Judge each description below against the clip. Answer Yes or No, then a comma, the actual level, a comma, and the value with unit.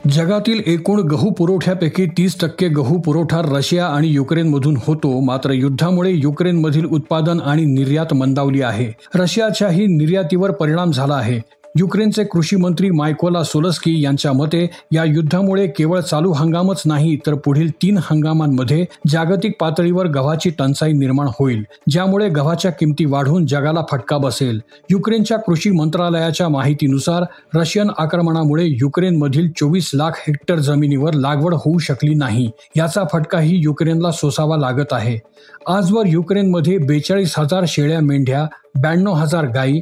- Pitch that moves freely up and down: No, average, 3.4 semitones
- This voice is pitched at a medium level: Yes, medium, 160 Hz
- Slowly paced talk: No, fast, 130 wpm